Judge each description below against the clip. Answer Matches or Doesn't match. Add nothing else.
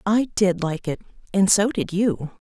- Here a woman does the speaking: Matches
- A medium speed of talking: Matches